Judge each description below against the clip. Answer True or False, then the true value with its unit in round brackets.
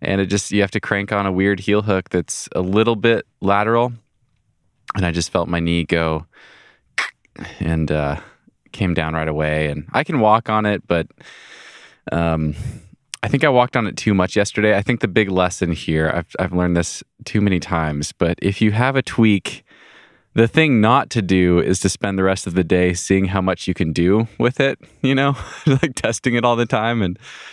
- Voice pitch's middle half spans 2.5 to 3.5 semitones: False (4.6 semitones)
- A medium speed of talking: False (210 wpm)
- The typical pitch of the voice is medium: False (100 Hz)